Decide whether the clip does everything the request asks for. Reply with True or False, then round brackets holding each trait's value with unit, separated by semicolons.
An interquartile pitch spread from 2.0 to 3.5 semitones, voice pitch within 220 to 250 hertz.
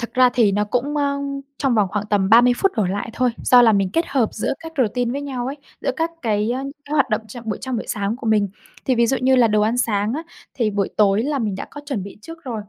False (4.0 semitones; 235 Hz)